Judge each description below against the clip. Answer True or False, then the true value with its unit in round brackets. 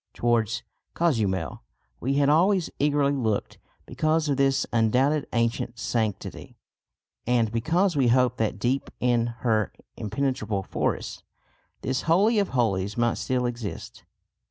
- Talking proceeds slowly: True (125 wpm)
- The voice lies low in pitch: True (125 Hz)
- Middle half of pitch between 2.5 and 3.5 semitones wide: False (4.0 semitones)